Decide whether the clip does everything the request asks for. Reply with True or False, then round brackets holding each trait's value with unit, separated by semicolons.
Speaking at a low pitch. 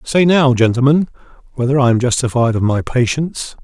True (130 Hz)